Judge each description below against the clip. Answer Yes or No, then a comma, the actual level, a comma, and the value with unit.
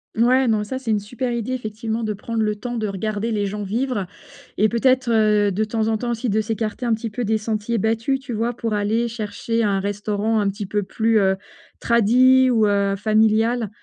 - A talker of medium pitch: No, high, 220 Hz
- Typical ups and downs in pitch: No, narrow, 2.1 semitones